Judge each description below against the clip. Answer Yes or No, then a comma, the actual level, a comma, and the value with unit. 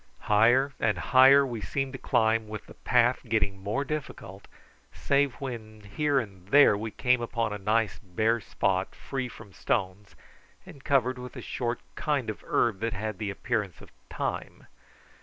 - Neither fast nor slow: Yes, average, 165 wpm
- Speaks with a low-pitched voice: Yes, low, 115 Hz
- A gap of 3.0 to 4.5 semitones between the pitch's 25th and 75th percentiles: Yes, average, 3.9 semitones